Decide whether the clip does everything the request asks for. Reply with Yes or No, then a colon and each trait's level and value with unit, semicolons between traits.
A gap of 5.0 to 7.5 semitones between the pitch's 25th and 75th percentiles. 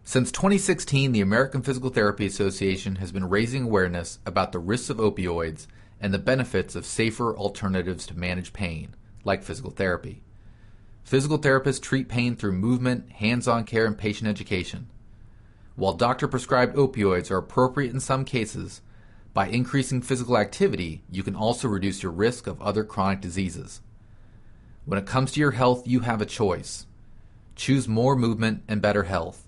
No: average, 4.1 semitones